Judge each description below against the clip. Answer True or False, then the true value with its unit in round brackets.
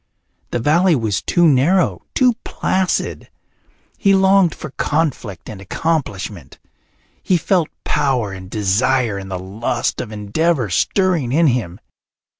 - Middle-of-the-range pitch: False (130 Hz)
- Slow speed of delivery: True (125 wpm)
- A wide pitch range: True (8.7 semitones)